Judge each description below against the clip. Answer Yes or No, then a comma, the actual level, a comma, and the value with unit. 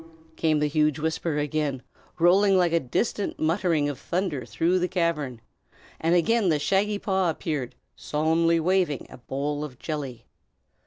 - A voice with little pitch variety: No, average, 3.4 semitones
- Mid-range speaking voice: Yes, medium, 160 Hz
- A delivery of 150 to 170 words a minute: Yes, average, 155 wpm